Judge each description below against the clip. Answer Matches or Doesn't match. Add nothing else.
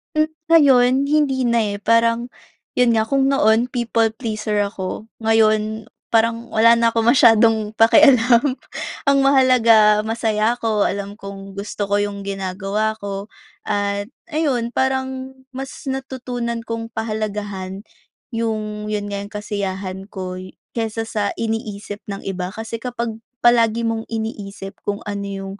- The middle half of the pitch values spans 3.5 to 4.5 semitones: Doesn't match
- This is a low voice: Doesn't match